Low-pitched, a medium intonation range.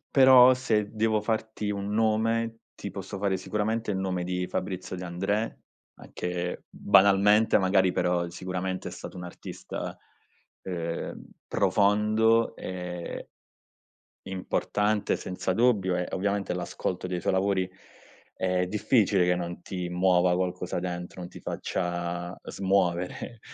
Yes: very low, 95 Hz; average, 3.0 semitones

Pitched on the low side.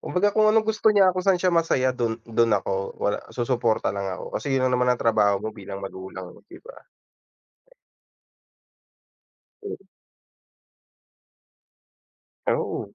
Yes: low, 125 Hz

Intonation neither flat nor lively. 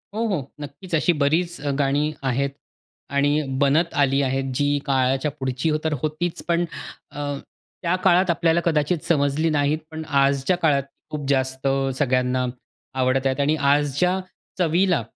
Yes: average, 3.3 semitones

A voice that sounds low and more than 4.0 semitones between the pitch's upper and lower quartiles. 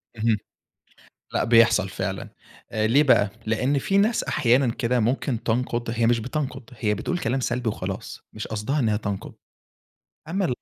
No: low, 120 Hz; average, 3.3 semitones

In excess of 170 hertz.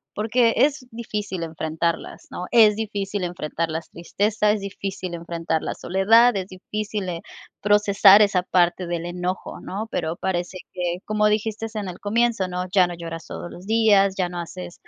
Yes: high, 190 Hz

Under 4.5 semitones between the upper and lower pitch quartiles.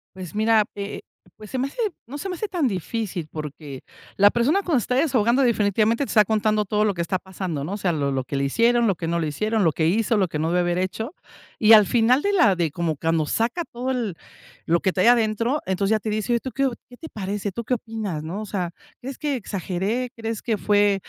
No: average, 4.8 semitones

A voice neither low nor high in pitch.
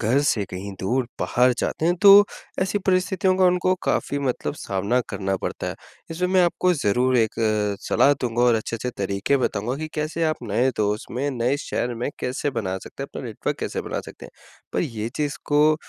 No: low, 130 Hz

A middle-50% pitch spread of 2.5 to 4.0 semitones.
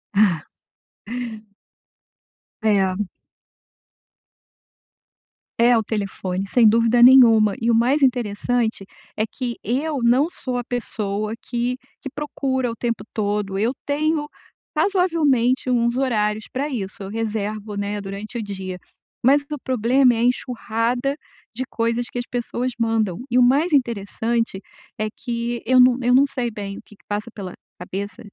Yes: average, 3.2 semitones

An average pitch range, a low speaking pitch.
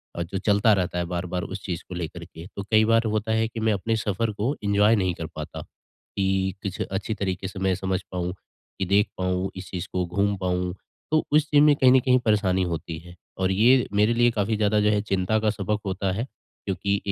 Yes: average, 3.1 semitones; low, 100 Hz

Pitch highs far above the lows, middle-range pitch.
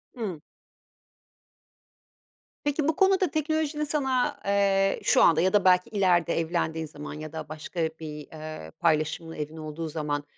Yes: wide, 7.9 semitones; medium, 170 Hz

